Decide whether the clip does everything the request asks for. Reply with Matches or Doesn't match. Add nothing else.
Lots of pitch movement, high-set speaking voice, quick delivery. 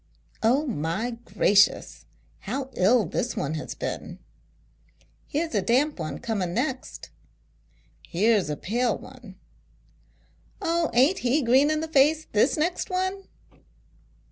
Doesn't match